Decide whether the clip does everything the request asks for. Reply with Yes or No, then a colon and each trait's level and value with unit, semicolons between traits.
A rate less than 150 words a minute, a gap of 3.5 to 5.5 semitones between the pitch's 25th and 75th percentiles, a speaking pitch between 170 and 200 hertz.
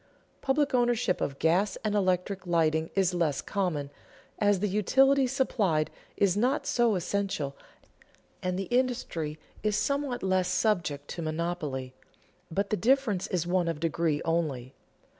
Yes: average, 140 wpm; average, 4.8 semitones; medium, 185 Hz